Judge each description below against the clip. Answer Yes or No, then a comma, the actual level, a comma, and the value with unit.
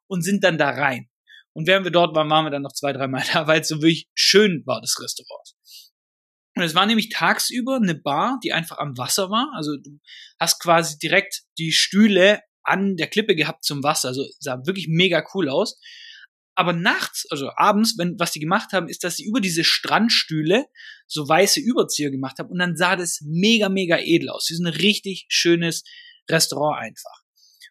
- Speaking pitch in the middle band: Yes, medium, 175 Hz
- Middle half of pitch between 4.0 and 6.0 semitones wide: Yes, average, 4.5 semitones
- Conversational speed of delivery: No, fast, 200 wpm